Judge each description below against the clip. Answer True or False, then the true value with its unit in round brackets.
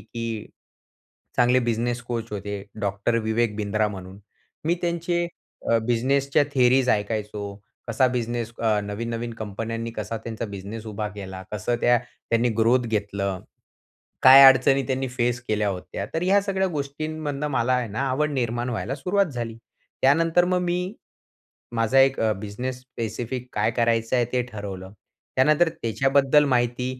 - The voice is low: True (120 Hz)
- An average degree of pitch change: True (3.8 semitones)